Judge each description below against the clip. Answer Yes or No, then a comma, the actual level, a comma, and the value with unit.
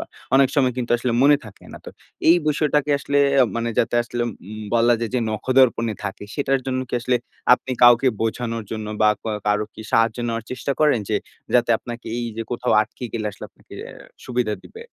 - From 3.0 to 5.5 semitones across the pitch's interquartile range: No, narrow, 2.4 semitones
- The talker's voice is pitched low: Yes, low, 120 Hz